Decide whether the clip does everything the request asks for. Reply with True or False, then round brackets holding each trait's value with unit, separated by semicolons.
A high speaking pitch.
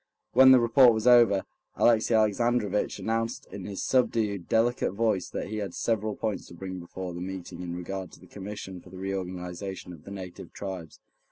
False (100 Hz)